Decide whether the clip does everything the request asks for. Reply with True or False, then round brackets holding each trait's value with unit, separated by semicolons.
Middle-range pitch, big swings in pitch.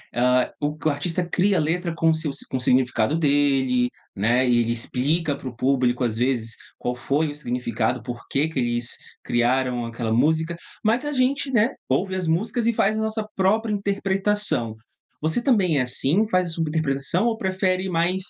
True (150 Hz; 7.1 semitones)